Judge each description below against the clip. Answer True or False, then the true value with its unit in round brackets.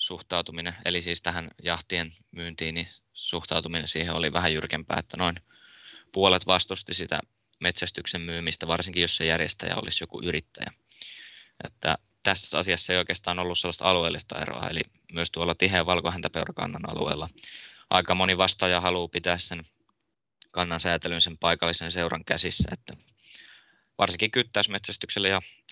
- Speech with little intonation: True (1.5 semitones)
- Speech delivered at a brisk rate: False (135 wpm)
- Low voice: True (85 Hz)